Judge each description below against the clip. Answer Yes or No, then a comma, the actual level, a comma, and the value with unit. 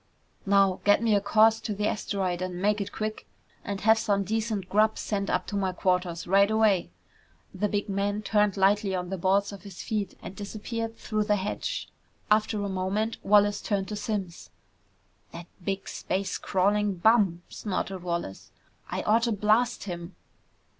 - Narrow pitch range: Yes, narrow, 1.9 semitones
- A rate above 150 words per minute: Yes, average, 165 wpm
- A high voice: Yes, high, 200 Hz